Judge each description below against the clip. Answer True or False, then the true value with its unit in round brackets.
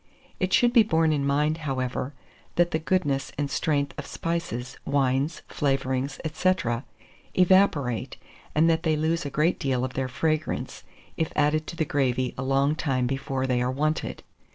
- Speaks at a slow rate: False (165 wpm)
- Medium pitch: True (145 Hz)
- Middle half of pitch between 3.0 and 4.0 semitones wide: True (3.4 semitones)